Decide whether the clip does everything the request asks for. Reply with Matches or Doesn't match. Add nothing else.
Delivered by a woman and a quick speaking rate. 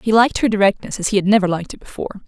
Matches